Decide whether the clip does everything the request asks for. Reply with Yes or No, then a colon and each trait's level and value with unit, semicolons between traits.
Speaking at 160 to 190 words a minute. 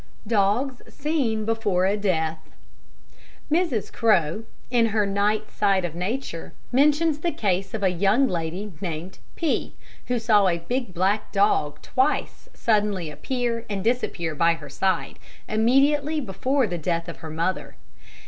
No: average, 140 wpm